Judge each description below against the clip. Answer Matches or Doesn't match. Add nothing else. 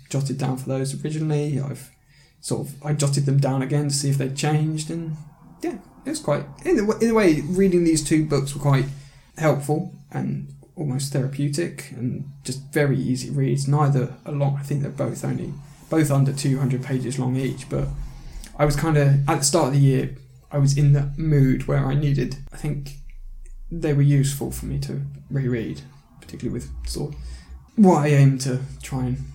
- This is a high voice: Doesn't match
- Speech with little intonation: Matches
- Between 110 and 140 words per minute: Doesn't match